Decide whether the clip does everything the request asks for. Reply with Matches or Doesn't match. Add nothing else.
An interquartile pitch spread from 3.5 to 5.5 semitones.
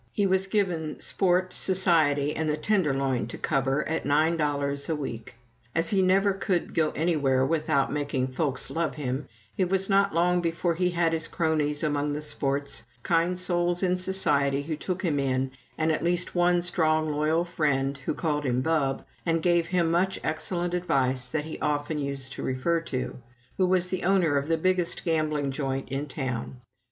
Matches